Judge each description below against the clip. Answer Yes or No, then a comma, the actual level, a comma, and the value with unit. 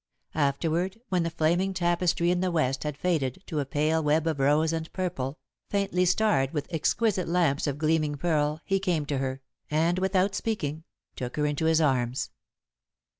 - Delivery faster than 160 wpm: Yes, average, 175 wpm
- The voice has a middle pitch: Yes, medium, 160 Hz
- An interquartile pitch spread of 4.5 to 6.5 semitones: No, average, 3.5 semitones